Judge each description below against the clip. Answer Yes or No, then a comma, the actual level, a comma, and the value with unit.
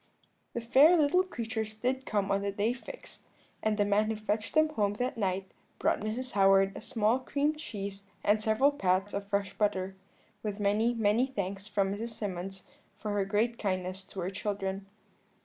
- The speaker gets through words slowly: No, average, 180 wpm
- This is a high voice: Yes, high, 210 Hz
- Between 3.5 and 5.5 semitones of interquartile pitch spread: No, average, 3.0 semitones